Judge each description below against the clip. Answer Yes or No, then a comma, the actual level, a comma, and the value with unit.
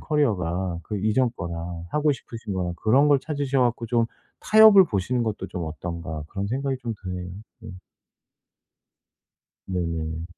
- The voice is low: Yes, low, 105 Hz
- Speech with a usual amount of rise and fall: No, wide, 7.1 semitones